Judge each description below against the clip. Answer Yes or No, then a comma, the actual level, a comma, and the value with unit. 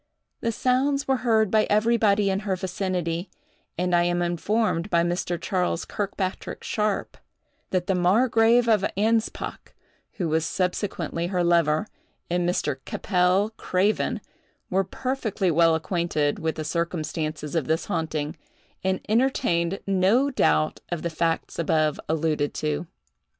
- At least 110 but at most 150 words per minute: Yes, slow, 135 wpm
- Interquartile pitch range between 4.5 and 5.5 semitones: No, average, 4.0 semitones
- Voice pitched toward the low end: No, medium, 180 Hz